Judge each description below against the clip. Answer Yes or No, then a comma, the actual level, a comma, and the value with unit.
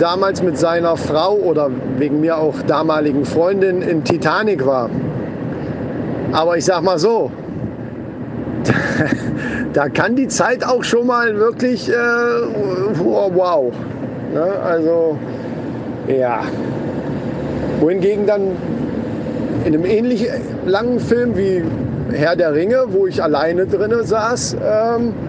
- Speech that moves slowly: Yes, slow, 110 wpm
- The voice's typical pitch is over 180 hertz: Yes, high, 190 Hz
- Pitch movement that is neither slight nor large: No, wide, 6.7 semitones